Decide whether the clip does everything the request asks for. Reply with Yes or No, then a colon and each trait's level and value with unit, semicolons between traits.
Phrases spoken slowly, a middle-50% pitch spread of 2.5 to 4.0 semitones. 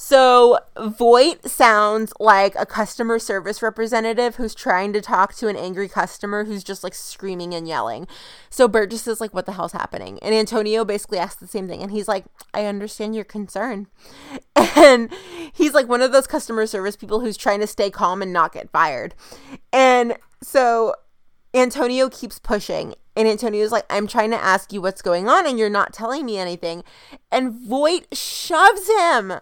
No: average, 180 wpm; average, 3.6 semitones